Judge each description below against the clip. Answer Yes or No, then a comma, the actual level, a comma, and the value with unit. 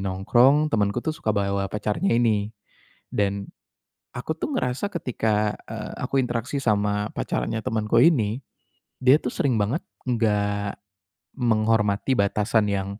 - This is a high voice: No, low, 110 Hz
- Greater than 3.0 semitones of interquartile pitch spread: Yes, average, 3.5 semitones